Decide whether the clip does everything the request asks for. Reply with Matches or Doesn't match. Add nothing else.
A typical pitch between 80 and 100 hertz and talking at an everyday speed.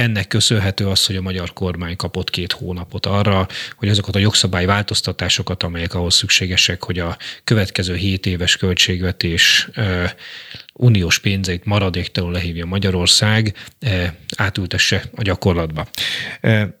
Matches